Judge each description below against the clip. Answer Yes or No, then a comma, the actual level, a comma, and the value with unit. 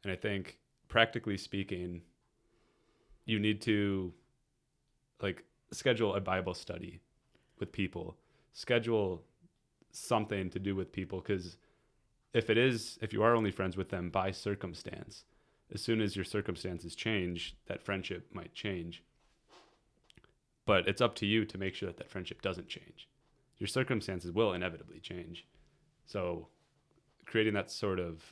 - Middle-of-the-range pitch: No, low, 100 Hz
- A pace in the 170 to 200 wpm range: No, average, 140 wpm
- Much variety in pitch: No, average, 4.0 semitones